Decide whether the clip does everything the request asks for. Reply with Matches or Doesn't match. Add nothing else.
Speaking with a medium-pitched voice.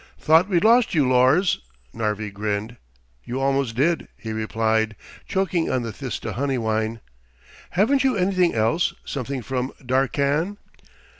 Doesn't match